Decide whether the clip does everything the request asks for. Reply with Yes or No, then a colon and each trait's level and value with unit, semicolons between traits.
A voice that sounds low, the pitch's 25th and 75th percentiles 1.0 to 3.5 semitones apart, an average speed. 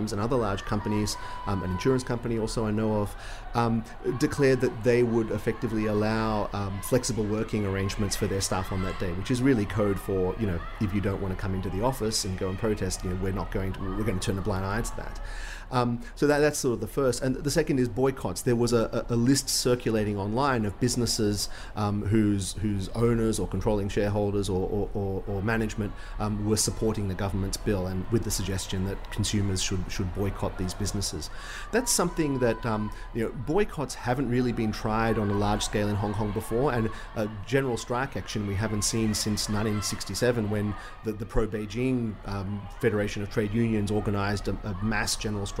No: low, 105 Hz; average, 2.8 semitones; fast, 210 wpm